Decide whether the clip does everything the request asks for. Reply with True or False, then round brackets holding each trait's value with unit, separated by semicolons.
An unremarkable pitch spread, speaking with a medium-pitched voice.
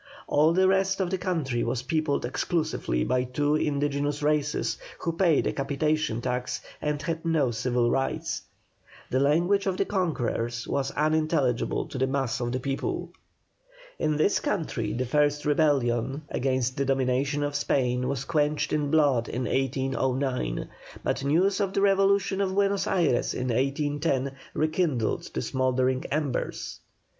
True (3.6 semitones; 145 Hz)